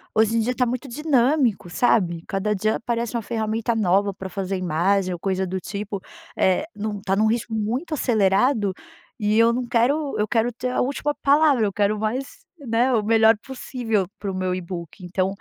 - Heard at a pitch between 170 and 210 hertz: No, high, 220 Hz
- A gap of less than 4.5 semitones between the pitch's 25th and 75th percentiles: Yes, average, 3.9 semitones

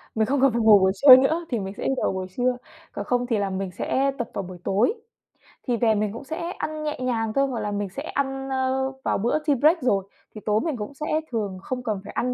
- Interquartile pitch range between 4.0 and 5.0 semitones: Yes, average, 4.6 semitones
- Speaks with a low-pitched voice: No, high, 240 Hz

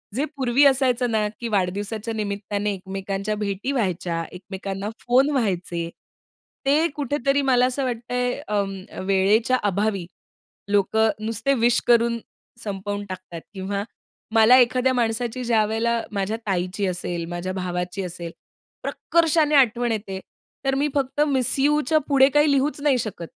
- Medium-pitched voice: No, high, 220 Hz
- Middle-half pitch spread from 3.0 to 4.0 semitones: No, average, 4.9 semitones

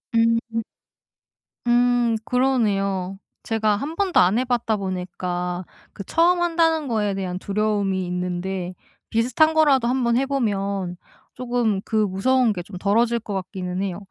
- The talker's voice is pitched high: Yes, high, 215 Hz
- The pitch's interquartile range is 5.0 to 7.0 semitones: No, average, 4.4 semitones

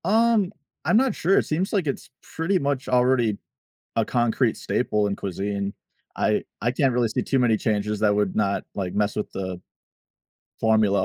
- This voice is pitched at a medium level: No, low, 115 Hz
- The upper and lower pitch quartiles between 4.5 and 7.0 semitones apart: Yes, wide, 5.6 semitones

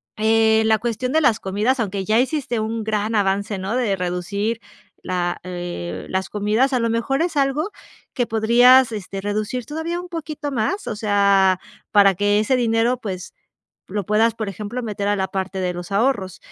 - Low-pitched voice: No, high, 215 Hz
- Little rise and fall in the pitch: No, average, 3.8 semitones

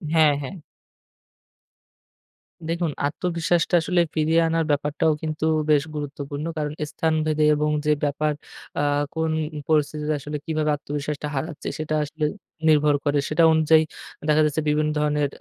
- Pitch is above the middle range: No, medium, 150 Hz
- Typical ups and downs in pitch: No, narrow, 1.2 semitones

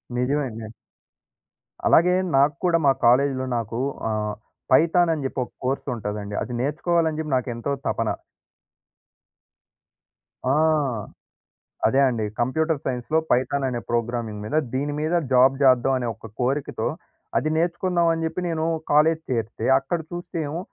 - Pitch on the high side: No, low, 135 Hz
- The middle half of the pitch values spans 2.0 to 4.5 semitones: No, average, 5.0 semitones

